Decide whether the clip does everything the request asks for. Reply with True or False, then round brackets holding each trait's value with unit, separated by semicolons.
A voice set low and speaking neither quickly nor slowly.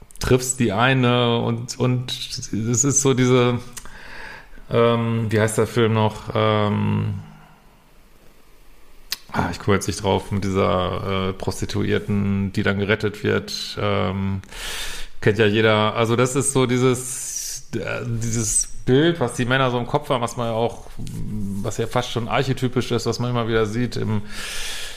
True (115 Hz; 155 wpm)